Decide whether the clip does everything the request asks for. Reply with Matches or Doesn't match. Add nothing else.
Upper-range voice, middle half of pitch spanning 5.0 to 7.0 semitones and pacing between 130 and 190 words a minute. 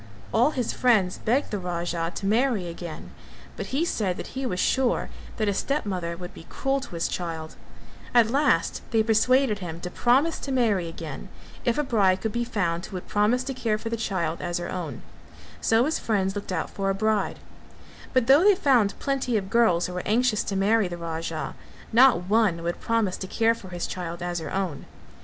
Doesn't match